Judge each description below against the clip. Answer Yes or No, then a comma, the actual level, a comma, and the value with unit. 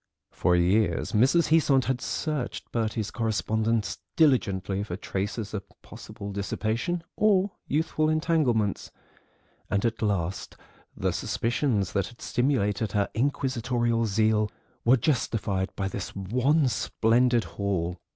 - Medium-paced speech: No, slow, 115 wpm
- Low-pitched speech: Yes, low, 115 Hz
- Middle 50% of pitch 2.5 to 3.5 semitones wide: No, average, 4.7 semitones